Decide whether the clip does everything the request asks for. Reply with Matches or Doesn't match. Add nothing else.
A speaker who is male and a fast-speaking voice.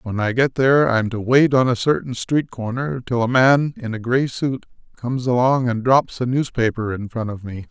Matches